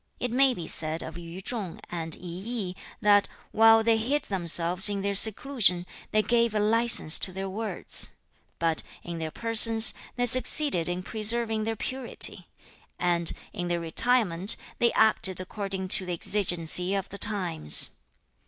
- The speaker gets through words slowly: No, average, 160 wpm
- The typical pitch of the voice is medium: No, high, 200 Hz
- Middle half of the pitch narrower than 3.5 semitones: No, average, 4.3 semitones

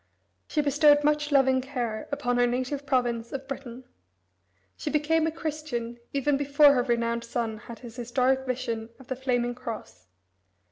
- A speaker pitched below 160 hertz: No, very high, 255 Hz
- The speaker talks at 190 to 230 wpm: No, average, 155 wpm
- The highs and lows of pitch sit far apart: No, average, 3.1 semitones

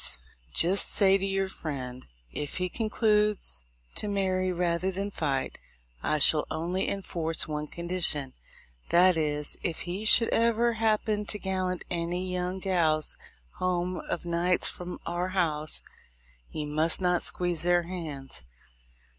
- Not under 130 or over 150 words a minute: Yes, average, 140 wpm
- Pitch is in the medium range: Yes, medium, 180 Hz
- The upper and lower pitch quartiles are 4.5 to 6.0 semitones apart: No, average, 3.2 semitones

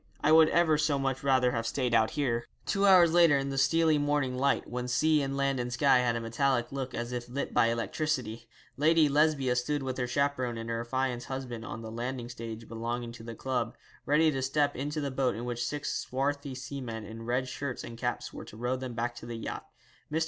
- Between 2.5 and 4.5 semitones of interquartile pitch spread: Yes, average, 3.1 semitones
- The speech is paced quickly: Yes, fast, 225 wpm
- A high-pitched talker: No, low, 130 Hz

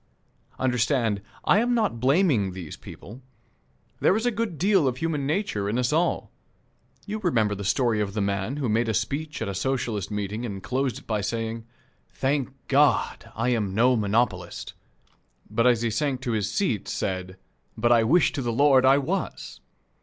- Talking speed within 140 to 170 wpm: No, average, 180 wpm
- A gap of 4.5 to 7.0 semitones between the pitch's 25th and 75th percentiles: Yes, average, 5.3 semitones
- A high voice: No, low, 120 Hz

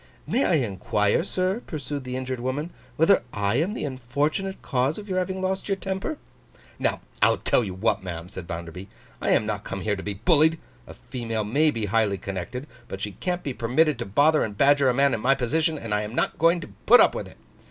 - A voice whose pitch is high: No, low, 130 Hz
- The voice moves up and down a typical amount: No, wide, 7.3 semitones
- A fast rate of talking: Yes, fast, 225 wpm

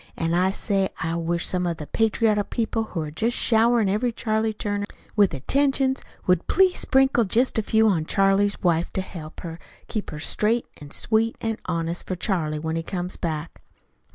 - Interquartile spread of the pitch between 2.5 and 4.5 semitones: No, average, 4.9 semitones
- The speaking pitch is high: Yes, high, 200 Hz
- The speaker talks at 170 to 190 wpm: Yes, average, 180 wpm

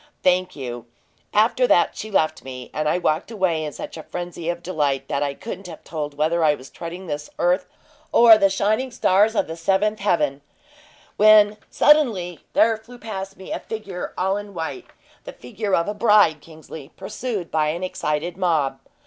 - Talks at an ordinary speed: Yes, average, 185 wpm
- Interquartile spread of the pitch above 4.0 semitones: Yes, average, 5.0 semitones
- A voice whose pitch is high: No, medium, 180 Hz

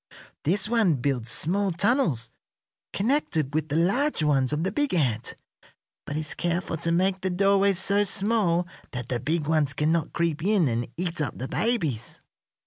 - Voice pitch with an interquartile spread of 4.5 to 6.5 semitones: Yes, average, 5.3 semitones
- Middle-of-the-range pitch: Yes, medium, 170 Hz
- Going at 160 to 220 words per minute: Yes, average, 165 wpm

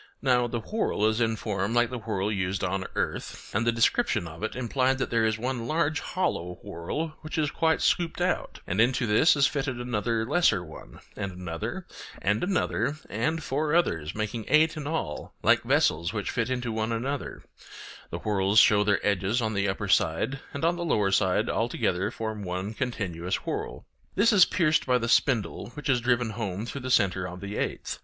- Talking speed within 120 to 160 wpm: No, average, 195 wpm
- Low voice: Yes, low, 115 Hz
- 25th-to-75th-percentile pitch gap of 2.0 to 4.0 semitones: No, wide, 5.4 semitones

